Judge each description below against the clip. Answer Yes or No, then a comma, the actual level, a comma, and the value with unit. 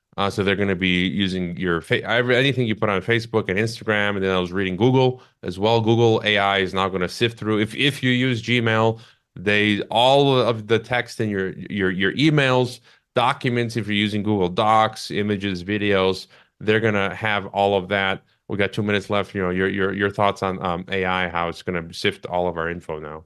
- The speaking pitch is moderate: No, low, 105 Hz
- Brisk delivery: Yes, fast, 220 wpm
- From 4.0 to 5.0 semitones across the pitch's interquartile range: No, average, 3.1 semitones